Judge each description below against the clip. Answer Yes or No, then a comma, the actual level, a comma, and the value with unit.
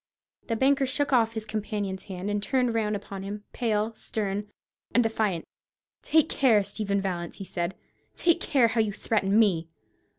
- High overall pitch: Yes, high, 215 Hz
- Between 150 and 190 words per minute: Yes, average, 165 wpm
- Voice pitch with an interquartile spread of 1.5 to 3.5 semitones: Yes, narrow, 2.6 semitones